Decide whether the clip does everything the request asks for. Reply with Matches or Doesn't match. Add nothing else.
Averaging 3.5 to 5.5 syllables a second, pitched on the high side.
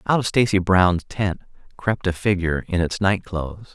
Doesn't match